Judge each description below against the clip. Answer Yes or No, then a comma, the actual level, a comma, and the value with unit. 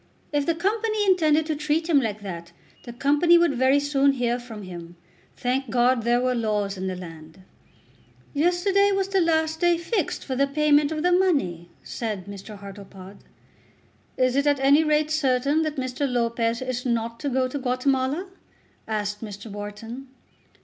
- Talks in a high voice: Yes, very high, 260 Hz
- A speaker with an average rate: Yes, average, 170 wpm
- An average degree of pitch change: No, wide, 5.7 semitones